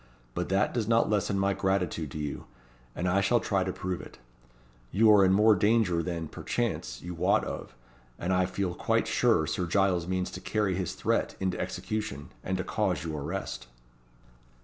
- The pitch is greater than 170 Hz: No, very low, 95 Hz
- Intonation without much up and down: Yes, narrow, 2.3 semitones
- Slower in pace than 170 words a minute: No, average, 185 wpm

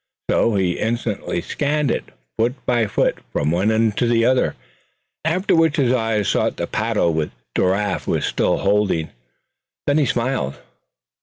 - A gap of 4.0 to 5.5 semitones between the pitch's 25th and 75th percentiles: Yes, average, 4.7 semitones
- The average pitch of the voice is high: No, low, 115 Hz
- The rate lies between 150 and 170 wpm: Yes, average, 155 wpm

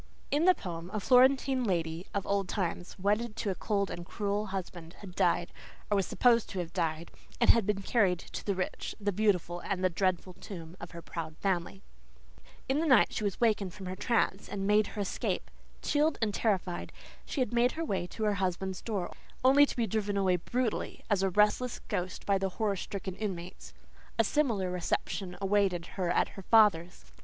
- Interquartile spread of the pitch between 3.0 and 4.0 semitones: Yes, average, 3.3 semitones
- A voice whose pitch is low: No, high, 195 Hz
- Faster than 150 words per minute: Yes, average, 190 wpm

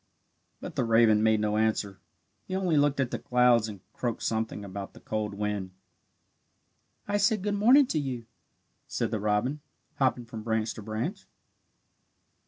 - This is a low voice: Yes, low, 115 Hz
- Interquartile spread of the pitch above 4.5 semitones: Yes, average, 4.9 semitones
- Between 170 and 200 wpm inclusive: No, average, 160 wpm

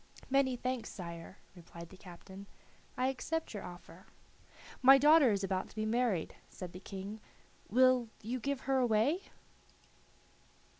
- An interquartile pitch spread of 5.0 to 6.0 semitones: Yes, wide, 5.4 semitones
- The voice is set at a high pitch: Yes, high, 220 Hz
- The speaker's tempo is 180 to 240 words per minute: No, average, 140 wpm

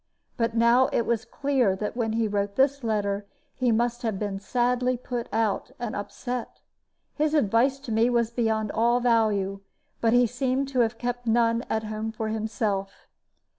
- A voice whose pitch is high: Yes, high, 230 Hz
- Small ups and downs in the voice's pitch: Yes, narrow, 2.2 semitones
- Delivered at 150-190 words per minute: Yes, average, 170 wpm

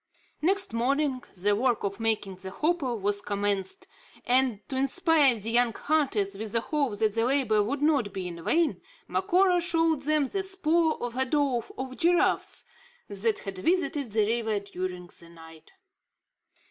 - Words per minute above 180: No, average, 160 wpm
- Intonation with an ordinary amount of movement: No, wide, 6.8 semitones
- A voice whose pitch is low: No, high, 240 Hz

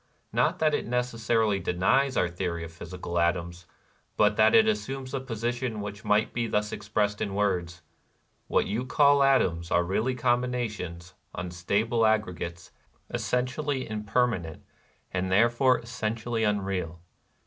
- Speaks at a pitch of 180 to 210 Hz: No, low, 105 Hz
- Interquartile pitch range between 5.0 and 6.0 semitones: Yes, wide, 5.5 semitones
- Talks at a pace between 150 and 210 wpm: No, slow, 135 wpm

